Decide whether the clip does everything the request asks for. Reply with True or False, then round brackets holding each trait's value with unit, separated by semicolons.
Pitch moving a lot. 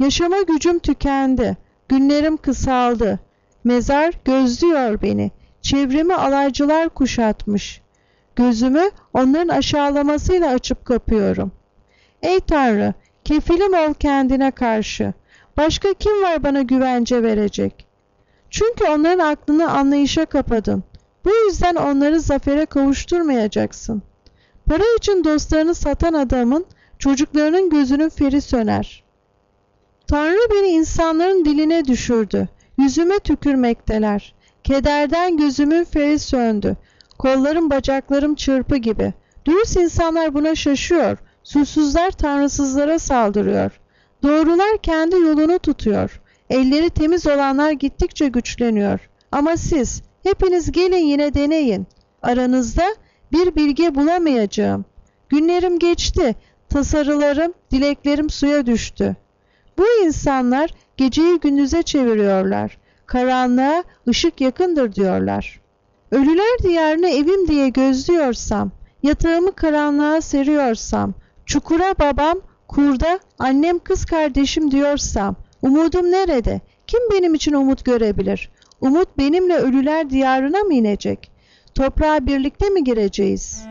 False (4.8 semitones)